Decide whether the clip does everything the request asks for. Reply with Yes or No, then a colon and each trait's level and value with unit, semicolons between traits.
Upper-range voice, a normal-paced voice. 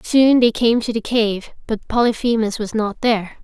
Yes: high, 225 Hz; average, 190 wpm